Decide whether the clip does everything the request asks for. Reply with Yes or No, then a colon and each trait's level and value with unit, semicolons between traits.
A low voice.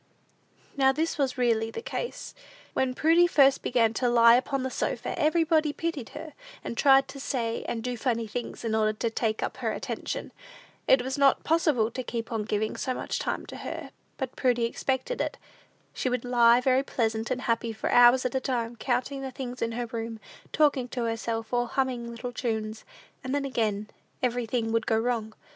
No: high, 245 Hz